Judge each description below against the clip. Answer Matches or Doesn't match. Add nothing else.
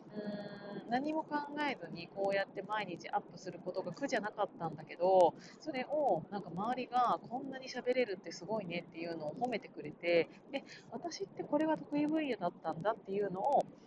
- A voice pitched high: Matches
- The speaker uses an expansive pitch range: Matches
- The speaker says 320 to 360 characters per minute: Doesn't match